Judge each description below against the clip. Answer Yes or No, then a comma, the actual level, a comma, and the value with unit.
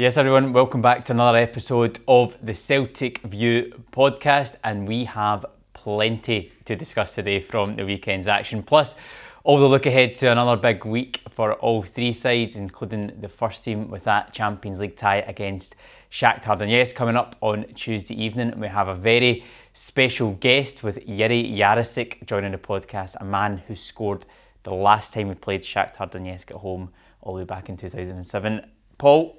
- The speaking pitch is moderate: No, low, 110 Hz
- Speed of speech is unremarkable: Yes, average, 180 wpm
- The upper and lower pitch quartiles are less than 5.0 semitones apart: Yes, average, 3.2 semitones